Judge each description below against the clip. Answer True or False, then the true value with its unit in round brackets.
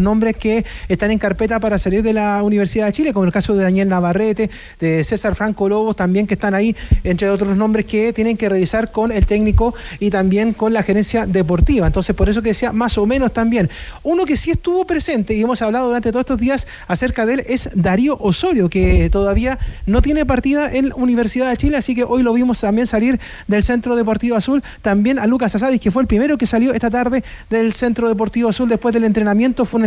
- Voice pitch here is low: False (225 Hz)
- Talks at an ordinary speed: False (220 wpm)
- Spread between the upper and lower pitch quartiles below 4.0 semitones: True (3.1 semitones)